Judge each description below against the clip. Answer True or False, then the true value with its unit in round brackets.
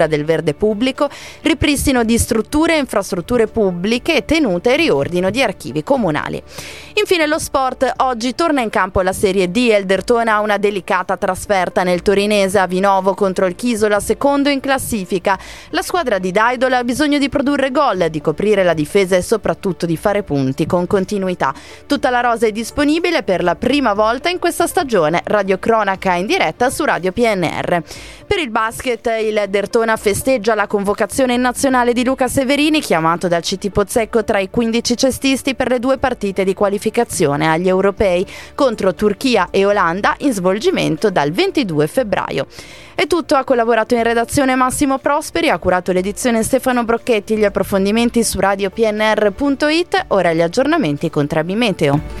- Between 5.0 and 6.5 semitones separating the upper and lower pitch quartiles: True (5.3 semitones)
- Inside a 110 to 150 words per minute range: False (160 wpm)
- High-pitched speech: True (220 Hz)